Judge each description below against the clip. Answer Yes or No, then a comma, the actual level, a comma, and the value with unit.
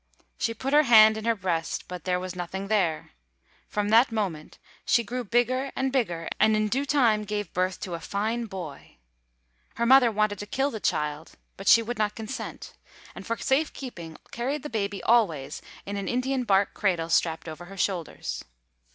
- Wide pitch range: No, average, 4.7 semitones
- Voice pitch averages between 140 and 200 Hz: No, high, 210 Hz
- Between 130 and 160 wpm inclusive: No, average, 185 wpm